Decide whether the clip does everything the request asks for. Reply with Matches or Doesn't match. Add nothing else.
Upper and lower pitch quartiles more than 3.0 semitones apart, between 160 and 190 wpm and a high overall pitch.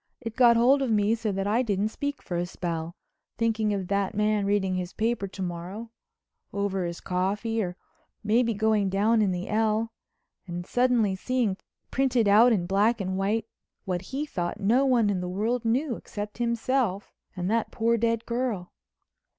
Matches